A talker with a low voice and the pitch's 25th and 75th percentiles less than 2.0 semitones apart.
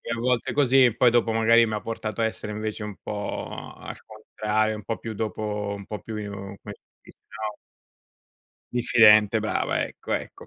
Yes: low, 110 Hz; narrow, 1.4 semitones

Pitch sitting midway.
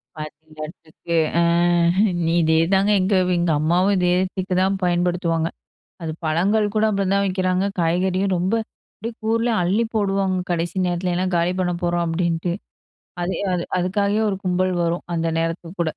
Yes: medium, 180 Hz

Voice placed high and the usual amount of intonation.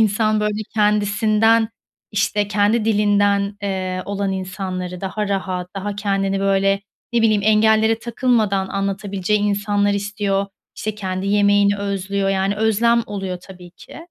No: high, 200 Hz; narrow, 1.4 semitones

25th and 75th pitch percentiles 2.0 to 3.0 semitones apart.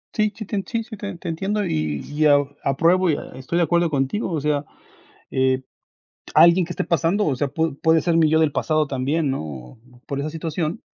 No: average, 3.7 semitones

